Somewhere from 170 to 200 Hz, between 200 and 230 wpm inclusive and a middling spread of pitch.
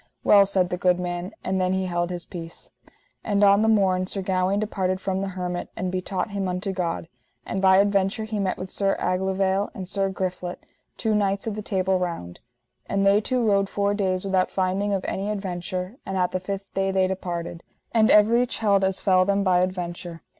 No: high, 190 Hz; fast, 205 wpm; narrow, 1.5 semitones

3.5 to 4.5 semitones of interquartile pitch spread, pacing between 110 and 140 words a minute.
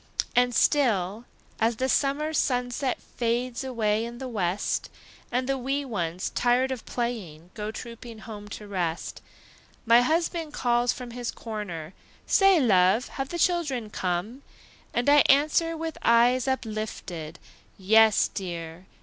Yes: average, 4.1 semitones; slow, 135 wpm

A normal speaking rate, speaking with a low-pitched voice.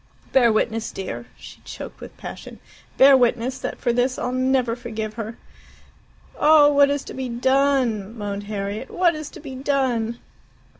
No: average, 160 wpm; high, 245 Hz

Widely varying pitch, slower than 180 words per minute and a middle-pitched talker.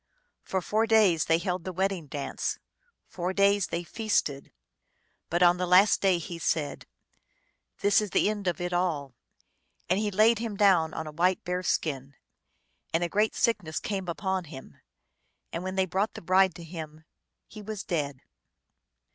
No: average, 3.3 semitones; average, 170 wpm; medium, 180 Hz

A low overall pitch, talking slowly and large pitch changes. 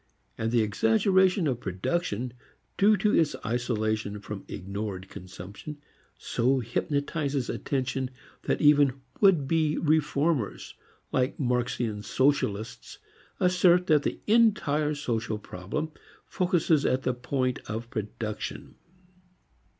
Yes: low, 130 Hz; slow, 105 wpm; wide, 6.0 semitones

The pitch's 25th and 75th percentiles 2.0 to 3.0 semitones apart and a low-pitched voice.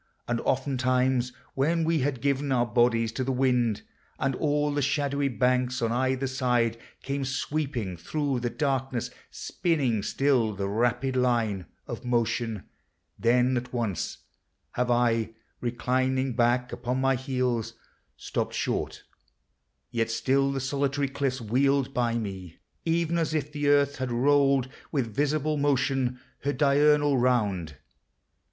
Yes: average, 2.7 semitones; low, 130 Hz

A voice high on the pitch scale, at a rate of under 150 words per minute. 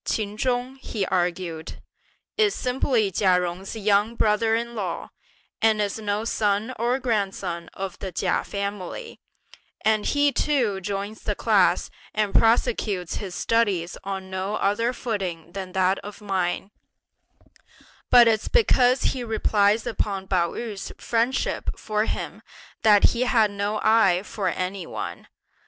Yes: high, 210 Hz; average, 140 wpm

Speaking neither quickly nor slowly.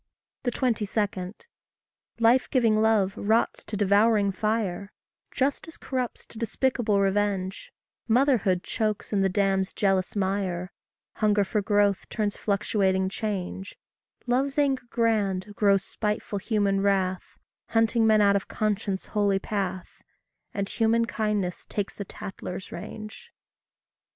No: slow, 115 wpm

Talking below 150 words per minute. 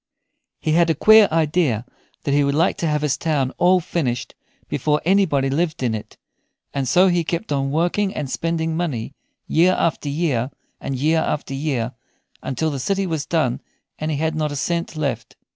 No: average, 185 wpm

